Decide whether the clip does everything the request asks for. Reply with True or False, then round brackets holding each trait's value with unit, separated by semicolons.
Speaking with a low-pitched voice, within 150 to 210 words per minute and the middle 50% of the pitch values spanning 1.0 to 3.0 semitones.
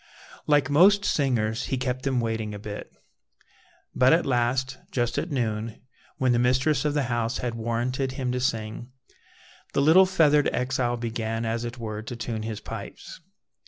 True (125 Hz; 165 wpm; 2.7 semitones)